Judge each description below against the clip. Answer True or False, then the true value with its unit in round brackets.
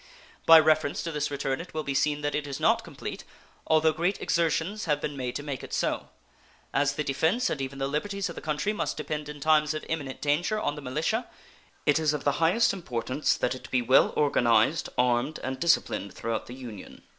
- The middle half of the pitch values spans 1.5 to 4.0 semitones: True (2.9 semitones)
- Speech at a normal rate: False (215 wpm)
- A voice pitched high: False (150 Hz)